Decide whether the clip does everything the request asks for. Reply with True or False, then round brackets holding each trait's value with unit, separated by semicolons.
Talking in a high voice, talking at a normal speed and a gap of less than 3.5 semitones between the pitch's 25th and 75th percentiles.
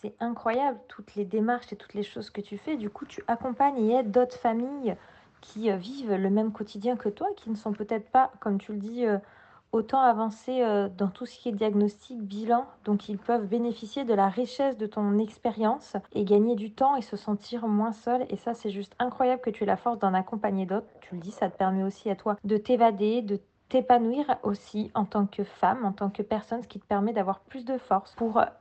False (220 Hz; 225 wpm; 2.8 semitones)